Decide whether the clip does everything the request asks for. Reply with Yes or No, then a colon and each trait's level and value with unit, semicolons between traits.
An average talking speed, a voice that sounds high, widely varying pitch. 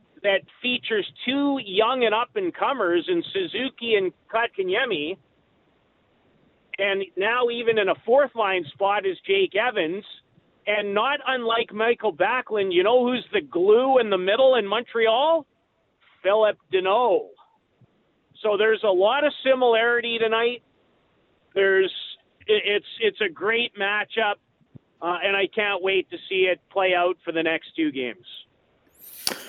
No: slow, 130 wpm; high, 230 Hz; wide, 7.1 semitones